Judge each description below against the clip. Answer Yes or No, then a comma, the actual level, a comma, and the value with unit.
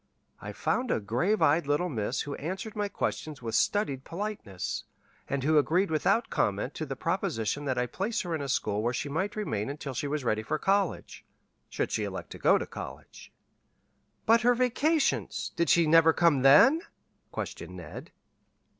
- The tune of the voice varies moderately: No, wide, 7.1 semitones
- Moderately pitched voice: Yes, medium, 155 Hz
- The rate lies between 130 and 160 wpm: No, average, 180 wpm